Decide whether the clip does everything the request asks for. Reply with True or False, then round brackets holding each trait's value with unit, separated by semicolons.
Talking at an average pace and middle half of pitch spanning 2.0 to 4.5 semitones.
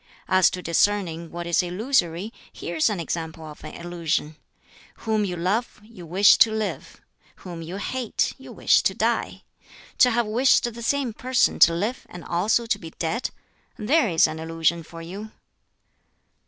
False (170 wpm; 4.9 semitones)